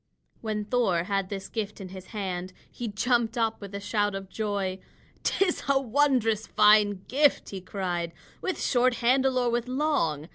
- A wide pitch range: No, average, 4.2 semitones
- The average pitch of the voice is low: No, high, 215 Hz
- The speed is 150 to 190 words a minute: Yes, average, 170 wpm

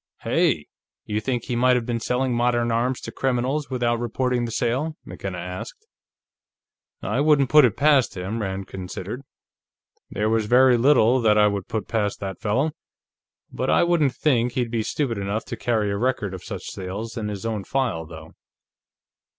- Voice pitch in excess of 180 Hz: No, low, 120 Hz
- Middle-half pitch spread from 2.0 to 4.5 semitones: Yes, average, 3.6 semitones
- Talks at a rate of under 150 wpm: No, average, 175 wpm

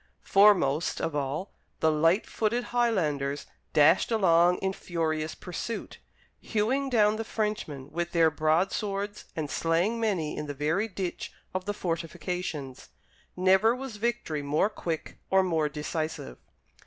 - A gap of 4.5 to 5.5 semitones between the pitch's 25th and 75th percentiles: Yes, average, 5.1 semitones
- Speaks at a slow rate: Yes, slow, 130 wpm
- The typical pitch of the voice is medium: Yes, medium, 175 Hz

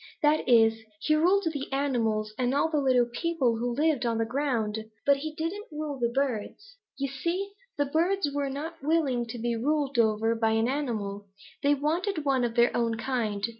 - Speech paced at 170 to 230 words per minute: Yes, average, 190 wpm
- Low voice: No, very high, 270 Hz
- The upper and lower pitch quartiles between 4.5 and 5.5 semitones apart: Yes, average, 4.8 semitones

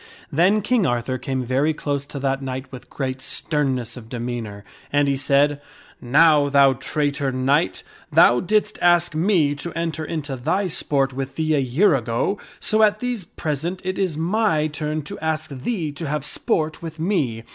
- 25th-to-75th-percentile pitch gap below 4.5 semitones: Yes, average, 3.8 semitones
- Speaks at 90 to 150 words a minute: No, average, 180 wpm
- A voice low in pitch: No, medium, 145 Hz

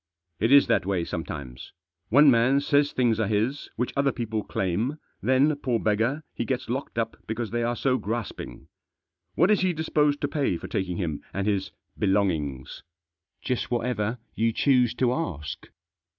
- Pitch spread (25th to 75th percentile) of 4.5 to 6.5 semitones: Yes, wide, 5.5 semitones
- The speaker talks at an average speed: Yes, average, 175 wpm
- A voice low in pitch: Yes, low, 115 Hz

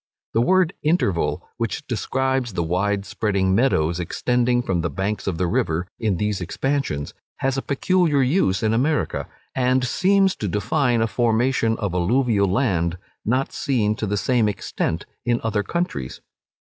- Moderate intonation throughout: No, wide, 5.7 semitones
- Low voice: Yes, low, 115 Hz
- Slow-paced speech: No, average, 155 wpm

